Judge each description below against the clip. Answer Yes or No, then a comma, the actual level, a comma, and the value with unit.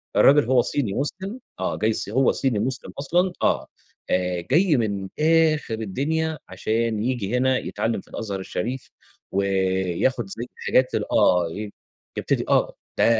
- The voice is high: No, low, 120 Hz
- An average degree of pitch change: No, wide, 6.1 semitones